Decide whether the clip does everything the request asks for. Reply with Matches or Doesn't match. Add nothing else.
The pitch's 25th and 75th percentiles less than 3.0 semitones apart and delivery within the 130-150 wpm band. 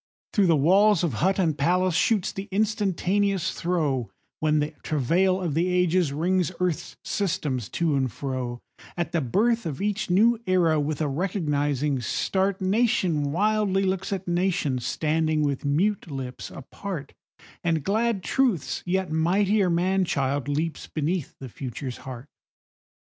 Doesn't match